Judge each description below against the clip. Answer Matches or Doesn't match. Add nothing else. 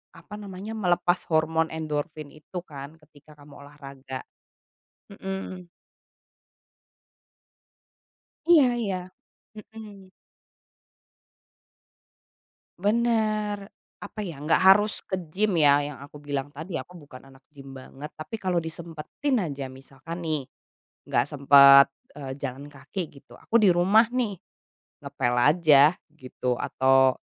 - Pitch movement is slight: Doesn't match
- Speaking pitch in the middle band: Matches